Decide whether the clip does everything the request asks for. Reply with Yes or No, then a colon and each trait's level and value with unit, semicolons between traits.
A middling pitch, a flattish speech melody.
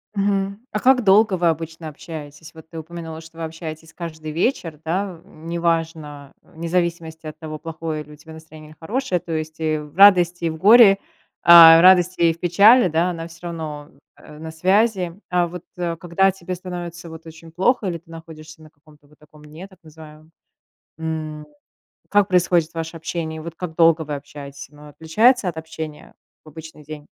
Yes: medium, 165 Hz; narrow, 2.1 semitones